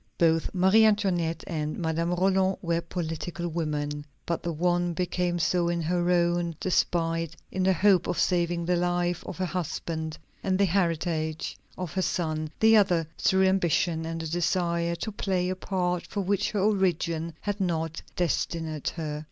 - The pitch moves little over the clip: Yes, narrow, 2.1 semitones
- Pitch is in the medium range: Yes, medium, 175 Hz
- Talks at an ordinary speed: Yes, average, 165 wpm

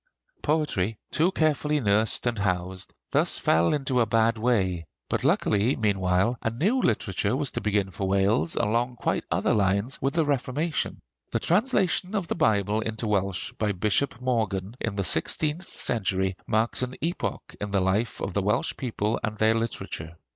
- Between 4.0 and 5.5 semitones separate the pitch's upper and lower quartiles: Yes, average, 5.2 semitones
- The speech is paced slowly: No, average, 170 wpm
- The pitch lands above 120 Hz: No, low, 110 Hz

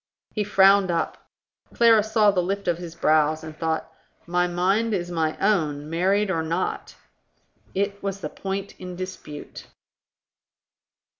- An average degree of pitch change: Yes, average, 3.3 semitones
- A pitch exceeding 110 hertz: Yes, medium, 185 Hz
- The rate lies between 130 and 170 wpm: Yes, average, 140 wpm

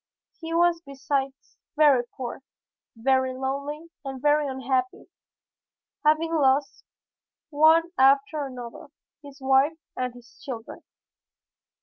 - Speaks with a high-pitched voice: Yes, very high, 275 Hz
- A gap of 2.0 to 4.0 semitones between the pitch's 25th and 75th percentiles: Yes, narrow, 2.5 semitones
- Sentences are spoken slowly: Yes, slow, 100 wpm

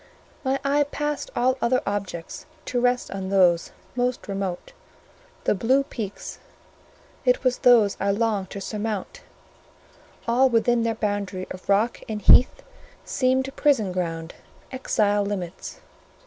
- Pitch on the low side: No, high, 220 Hz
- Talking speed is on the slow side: Yes, slow, 130 wpm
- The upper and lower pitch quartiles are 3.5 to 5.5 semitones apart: Yes, average, 4.4 semitones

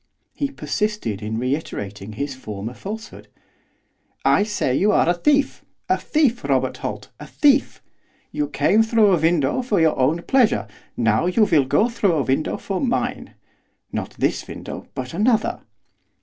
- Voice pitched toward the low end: No, medium, 180 Hz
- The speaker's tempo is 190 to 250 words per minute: No, average, 155 wpm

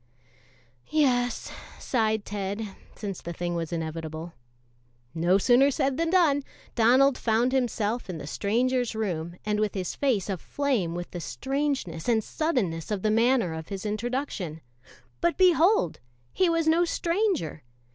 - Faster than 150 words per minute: No, average, 140 wpm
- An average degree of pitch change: No, wide, 7.5 semitones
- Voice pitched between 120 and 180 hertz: No, high, 220 Hz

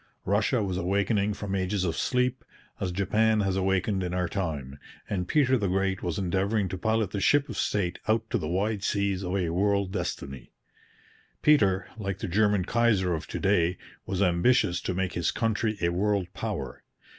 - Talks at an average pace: Yes, average, 180 wpm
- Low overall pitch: Yes, very low, 95 Hz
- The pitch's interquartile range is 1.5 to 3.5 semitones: Yes, average, 2.7 semitones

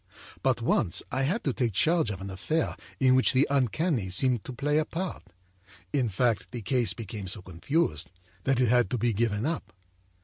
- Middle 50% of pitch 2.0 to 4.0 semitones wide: No, average, 5.1 semitones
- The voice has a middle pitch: No, low, 125 Hz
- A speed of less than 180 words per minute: No, average, 195 wpm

